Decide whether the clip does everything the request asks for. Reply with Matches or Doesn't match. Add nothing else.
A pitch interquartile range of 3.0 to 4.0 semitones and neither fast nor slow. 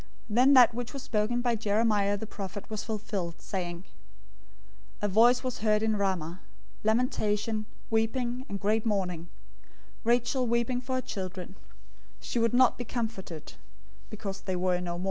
Matches